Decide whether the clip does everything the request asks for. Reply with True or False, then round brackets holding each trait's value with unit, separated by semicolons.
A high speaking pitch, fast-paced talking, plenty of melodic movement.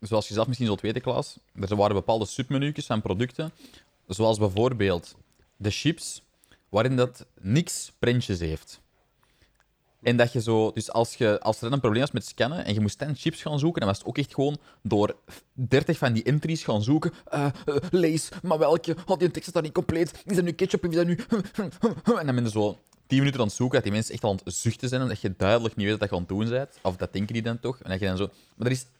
False (120 Hz; 245 wpm; 5.8 semitones)